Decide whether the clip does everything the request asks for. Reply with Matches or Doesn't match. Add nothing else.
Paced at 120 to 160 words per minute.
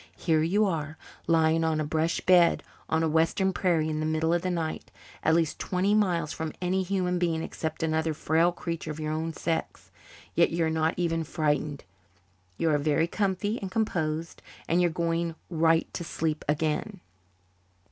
Doesn't match